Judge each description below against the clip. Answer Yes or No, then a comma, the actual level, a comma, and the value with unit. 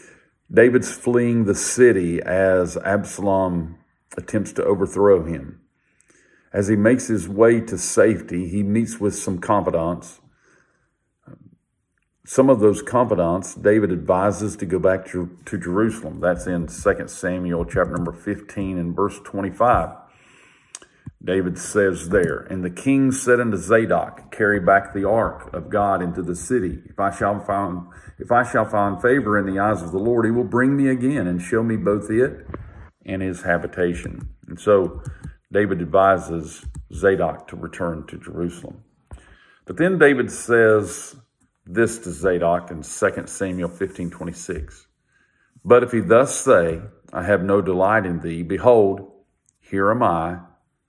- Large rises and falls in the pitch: No, average, 3.8 semitones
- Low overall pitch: Yes, very low, 95 Hz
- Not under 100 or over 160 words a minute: Yes, average, 145 wpm